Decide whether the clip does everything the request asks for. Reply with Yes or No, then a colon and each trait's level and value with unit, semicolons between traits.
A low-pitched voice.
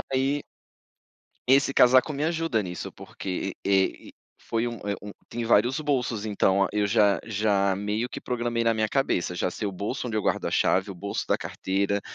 Yes: low, 110 Hz